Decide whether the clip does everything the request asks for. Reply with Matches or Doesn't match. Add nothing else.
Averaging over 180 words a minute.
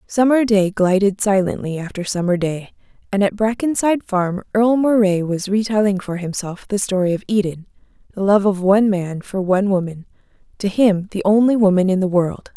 Doesn't match